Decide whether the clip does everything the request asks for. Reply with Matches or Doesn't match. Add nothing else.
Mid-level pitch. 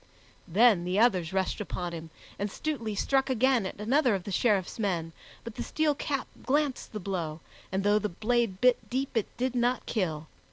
Doesn't match